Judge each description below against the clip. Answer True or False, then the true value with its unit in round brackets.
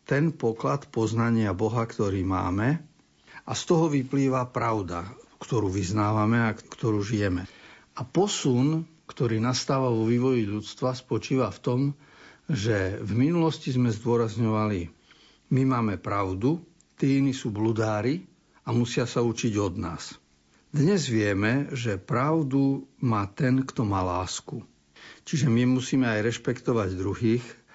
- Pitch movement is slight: False (4.3 semitones)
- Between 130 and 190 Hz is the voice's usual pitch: False (120 Hz)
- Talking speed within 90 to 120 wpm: False (130 wpm)